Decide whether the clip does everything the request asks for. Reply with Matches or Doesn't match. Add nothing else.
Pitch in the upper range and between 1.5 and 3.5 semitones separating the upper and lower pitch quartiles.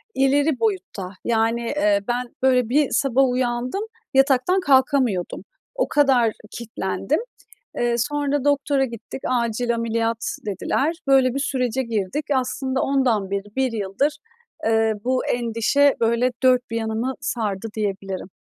Matches